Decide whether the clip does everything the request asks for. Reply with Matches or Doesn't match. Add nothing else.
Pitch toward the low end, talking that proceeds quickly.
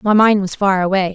Doesn't match